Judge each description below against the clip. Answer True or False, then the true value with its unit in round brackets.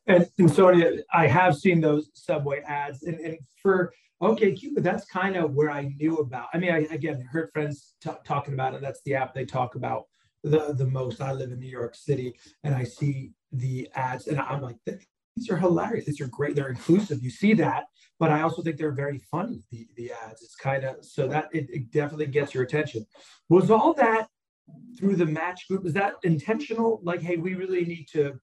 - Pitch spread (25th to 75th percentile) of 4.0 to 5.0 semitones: True (4.7 semitones)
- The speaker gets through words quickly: True (215 wpm)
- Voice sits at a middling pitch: True (150 Hz)